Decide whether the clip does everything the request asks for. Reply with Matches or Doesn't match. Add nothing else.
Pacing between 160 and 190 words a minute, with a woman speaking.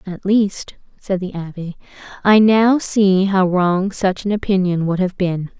Matches